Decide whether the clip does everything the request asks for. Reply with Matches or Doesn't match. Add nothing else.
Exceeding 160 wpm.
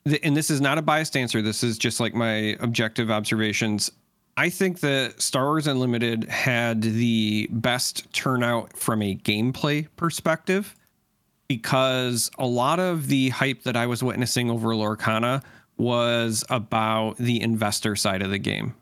Doesn't match